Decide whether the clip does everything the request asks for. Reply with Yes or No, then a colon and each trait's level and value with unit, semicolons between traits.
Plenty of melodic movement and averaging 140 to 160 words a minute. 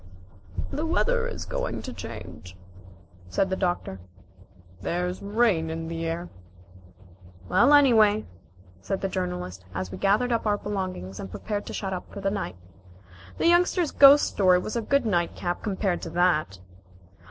Yes: wide, 5.8 semitones; average, 155 wpm